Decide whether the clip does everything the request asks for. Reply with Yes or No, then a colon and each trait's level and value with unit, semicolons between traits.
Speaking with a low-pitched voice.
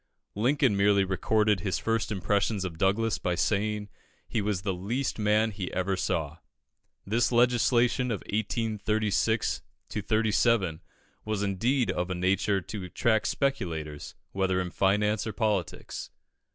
Yes: low, 105 Hz